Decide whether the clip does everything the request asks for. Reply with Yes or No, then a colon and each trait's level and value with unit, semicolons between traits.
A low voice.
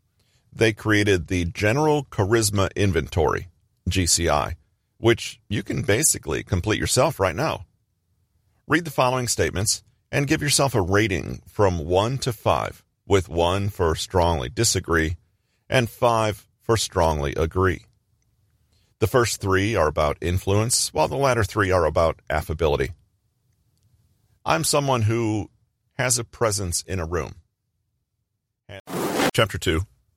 Yes: low, 105 Hz